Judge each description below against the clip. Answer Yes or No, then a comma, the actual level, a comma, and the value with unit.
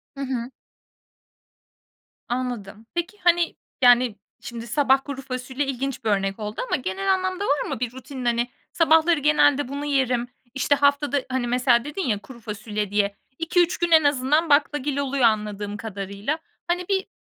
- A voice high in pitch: Yes, very high, 260 Hz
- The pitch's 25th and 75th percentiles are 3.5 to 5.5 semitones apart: Yes, average, 4.0 semitones